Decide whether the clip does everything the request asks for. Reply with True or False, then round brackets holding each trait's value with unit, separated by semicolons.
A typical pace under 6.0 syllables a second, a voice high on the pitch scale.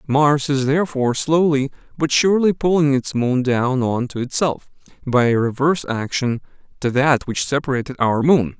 False (5.0 syllables/s; 135 Hz)